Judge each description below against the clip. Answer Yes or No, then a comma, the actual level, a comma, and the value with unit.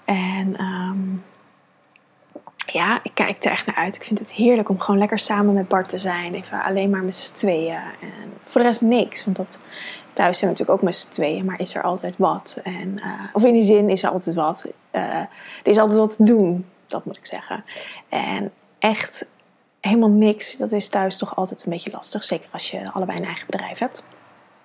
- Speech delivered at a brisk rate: Yes, fast, 215 wpm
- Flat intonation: Yes, narrow, 2.3 semitones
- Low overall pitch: No, high, 200 Hz